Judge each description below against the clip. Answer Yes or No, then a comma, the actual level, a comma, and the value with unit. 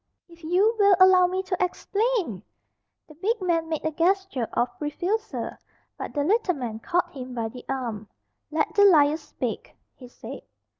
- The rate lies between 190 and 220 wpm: No, average, 165 wpm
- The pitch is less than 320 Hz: No, very high, 335 Hz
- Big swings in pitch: Yes, wide, 5.9 semitones